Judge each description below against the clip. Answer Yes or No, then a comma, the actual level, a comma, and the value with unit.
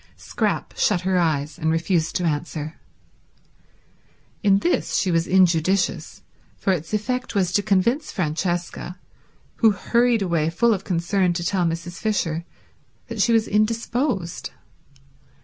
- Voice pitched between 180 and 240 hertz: Yes, medium, 185 Hz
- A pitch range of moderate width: Yes, average, 4.0 semitones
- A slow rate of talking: Yes, slow, 130 wpm